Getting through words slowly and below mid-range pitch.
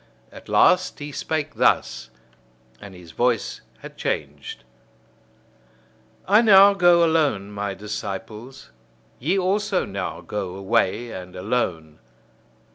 Yes: slow, 110 wpm; low, 115 Hz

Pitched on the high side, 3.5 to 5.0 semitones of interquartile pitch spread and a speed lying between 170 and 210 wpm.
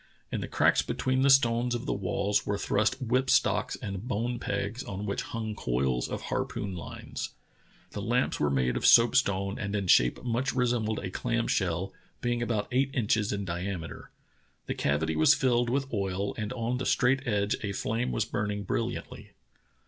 No: low, 105 Hz; average, 3.8 semitones; average, 180 wpm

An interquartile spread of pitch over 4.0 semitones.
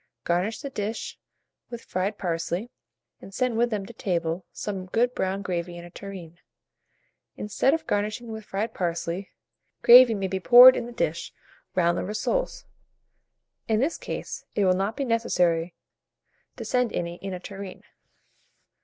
Yes: average, 4.5 semitones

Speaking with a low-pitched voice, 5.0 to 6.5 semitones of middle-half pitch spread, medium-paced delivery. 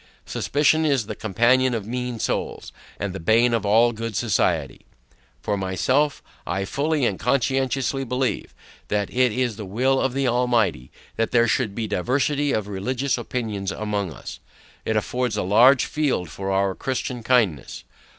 No: low, 120 Hz; average, 4.0 semitones; average, 160 wpm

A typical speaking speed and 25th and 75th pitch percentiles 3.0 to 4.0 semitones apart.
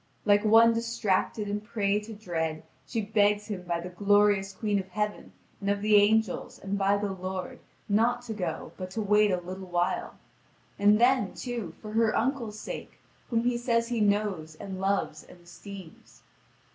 No: average, 175 wpm; narrow, 2.6 semitones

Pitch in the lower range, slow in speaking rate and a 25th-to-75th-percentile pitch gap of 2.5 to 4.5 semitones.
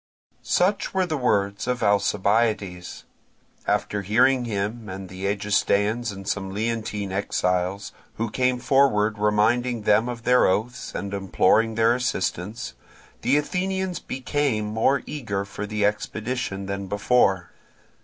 Yes: low, 105 Hz; slow, 125 wpm; average, 3.7 semitones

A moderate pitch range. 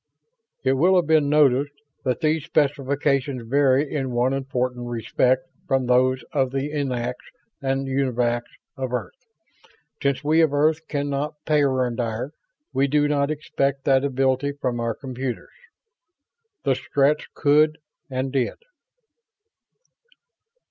No: narrow, 2.2 semitones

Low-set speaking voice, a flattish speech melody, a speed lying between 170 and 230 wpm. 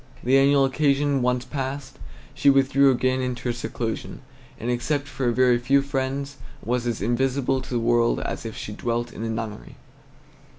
Yes: low, 130 Hz; narrow, 2.3 semitones; average, 180 wpm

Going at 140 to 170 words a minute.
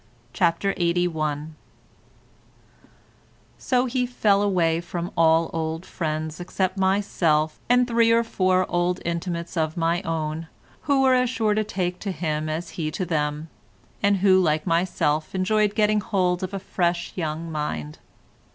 Yes: average, 145 wpm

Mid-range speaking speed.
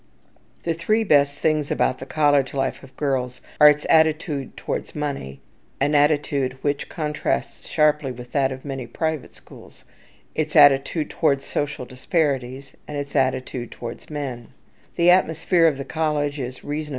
No: slow, 125 wpm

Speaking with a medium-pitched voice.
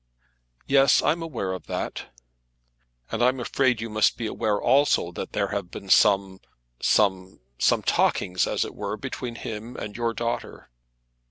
No: low, 110 Hz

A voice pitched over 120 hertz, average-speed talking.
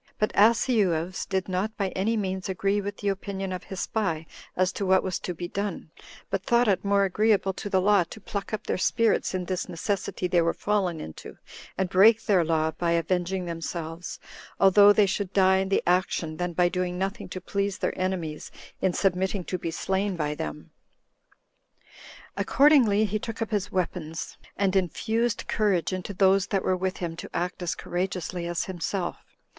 Yes: high, 190 Hz; average, 185 wpm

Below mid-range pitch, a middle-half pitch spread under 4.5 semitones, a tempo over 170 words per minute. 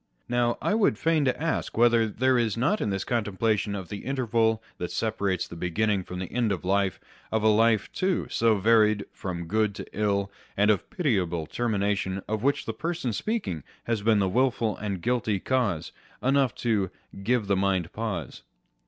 Yes: low, 110 Hz; average, 3.5 semitones; average, 185 wpm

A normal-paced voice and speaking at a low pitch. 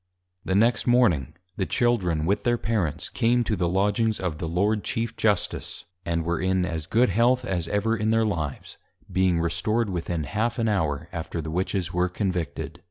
Yes: average, 180 wpm; very low, 95 Hz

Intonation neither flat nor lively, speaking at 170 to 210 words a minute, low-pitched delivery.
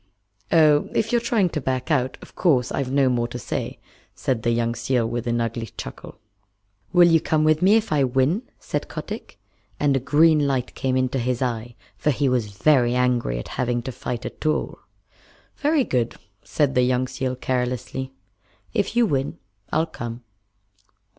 Yes: average, 4.0 semitones; average, 180 wpm; low, 130 Hz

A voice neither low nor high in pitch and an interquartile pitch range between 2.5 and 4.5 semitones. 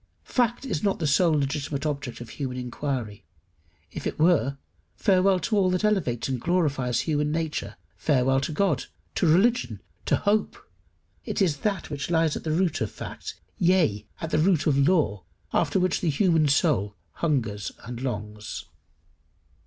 No: medium, 150 Hz; average, 5.3 semitones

